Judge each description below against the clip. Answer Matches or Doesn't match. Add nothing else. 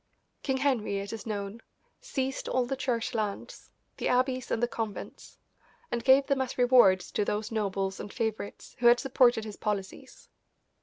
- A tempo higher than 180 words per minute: Doesn't match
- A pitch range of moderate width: Matches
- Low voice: Doesn't match